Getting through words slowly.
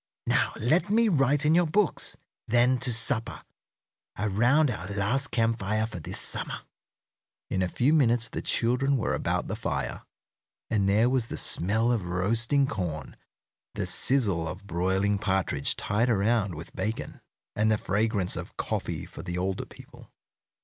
No: average, 155 wpm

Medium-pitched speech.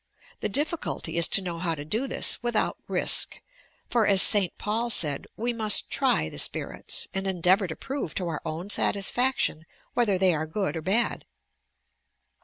No: high, 195 Hz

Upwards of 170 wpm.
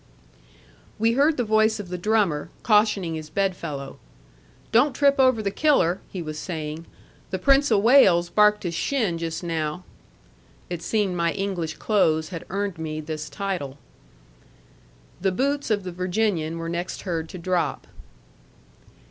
No: average, 150 wpm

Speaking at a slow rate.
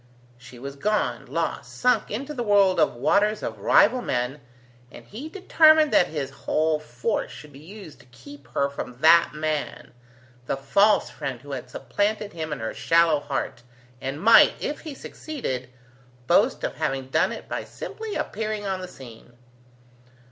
No: average, 165 wpm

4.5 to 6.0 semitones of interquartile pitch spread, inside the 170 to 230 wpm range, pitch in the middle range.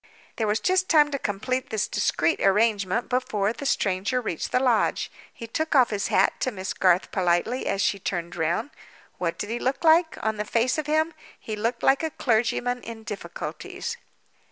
No: average, 4.8 semitones; average, 185 wpm; high, 230 Hz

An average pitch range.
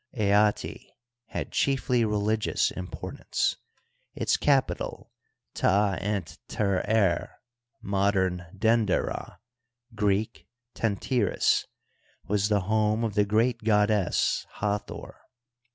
No: narrow, 1.8 semitones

